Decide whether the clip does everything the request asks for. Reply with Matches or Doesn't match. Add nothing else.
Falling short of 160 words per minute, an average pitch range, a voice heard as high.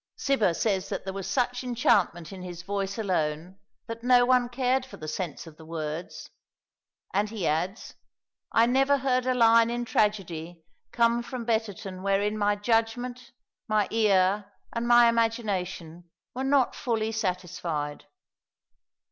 Matches